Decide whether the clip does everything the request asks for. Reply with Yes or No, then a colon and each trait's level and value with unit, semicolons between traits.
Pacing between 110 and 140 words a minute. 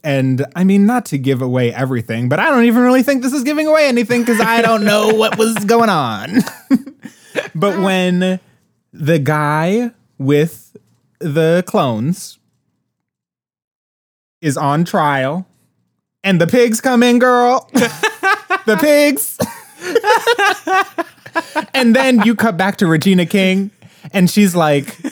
Yes: slow, 135 wpm